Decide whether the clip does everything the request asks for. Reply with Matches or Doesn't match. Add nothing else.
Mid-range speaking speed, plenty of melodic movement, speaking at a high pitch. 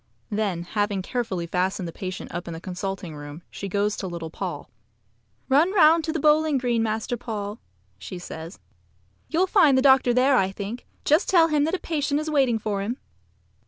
Matches